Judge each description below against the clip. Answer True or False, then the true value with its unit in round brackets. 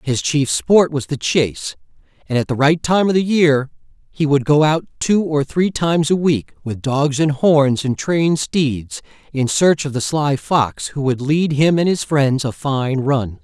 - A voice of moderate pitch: True (145 Hz)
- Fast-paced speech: True (210 wpm)